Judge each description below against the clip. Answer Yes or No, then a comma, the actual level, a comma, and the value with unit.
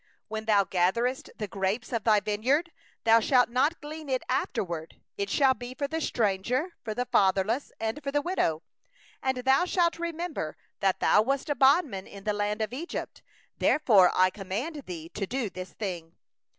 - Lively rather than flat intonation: Yes, wide, 6.0 semitones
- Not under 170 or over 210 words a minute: Yes, average, 180 wpm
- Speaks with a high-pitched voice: Yes, high, 225 Hz